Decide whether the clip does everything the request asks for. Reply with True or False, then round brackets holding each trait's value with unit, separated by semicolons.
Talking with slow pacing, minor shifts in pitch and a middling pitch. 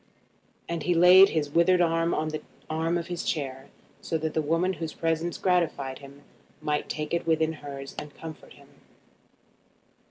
False (165 wpm; 2.2 semitones; 160 Hz)